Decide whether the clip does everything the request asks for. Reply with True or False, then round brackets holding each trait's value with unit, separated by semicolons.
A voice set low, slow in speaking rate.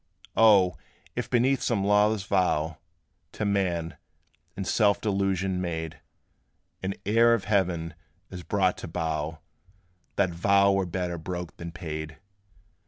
True (95 Hz; 125 wpm)